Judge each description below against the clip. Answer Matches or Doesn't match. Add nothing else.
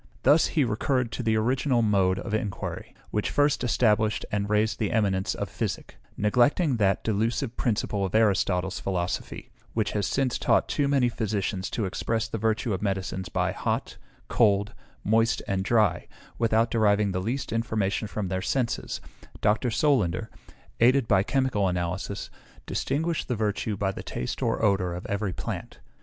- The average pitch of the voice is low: Matches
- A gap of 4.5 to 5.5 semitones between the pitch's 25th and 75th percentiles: Doesn't match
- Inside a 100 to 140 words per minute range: Doesn't match